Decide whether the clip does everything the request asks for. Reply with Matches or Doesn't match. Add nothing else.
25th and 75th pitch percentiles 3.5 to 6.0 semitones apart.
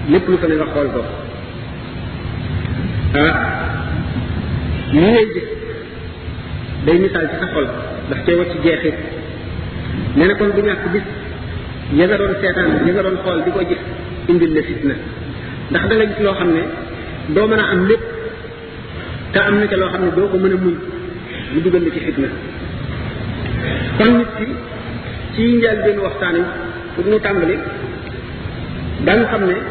Matches